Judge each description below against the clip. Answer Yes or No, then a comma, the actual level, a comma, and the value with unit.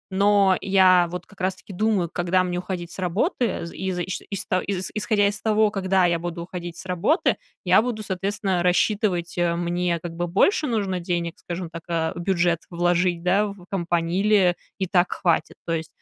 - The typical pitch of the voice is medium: Yes, medium, 180 Hz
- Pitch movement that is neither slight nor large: No, narrow, 2.3 semitones